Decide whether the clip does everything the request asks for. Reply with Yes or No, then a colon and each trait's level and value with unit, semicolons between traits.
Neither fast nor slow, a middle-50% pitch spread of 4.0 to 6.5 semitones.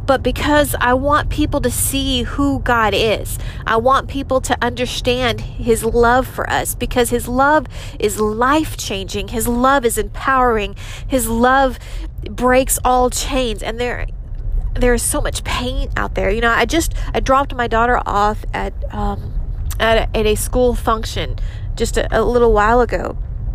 No: average, 170 wpm; average, 3.3 semitones